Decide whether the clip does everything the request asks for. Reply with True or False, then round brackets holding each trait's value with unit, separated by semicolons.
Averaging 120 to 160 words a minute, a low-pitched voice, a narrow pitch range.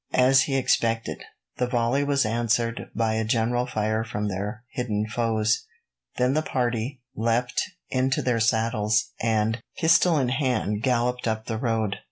True (150 wpm; 115 Hz; 2.2 semitones)